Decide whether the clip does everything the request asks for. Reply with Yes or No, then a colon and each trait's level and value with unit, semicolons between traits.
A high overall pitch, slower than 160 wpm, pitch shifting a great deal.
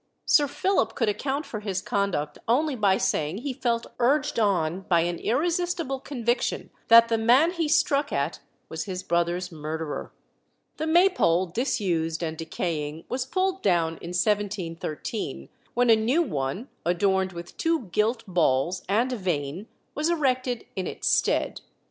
Yes: high, 210 Hz; average, 150 wpm; wide, 7.5 semitones